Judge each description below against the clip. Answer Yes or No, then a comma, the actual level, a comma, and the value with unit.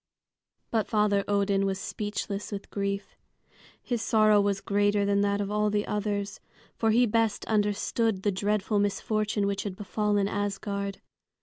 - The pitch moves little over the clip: Yes, narrow, 1.0 semitones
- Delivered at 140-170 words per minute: Yes, average, 145 wpm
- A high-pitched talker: Yes, high, 205 Hz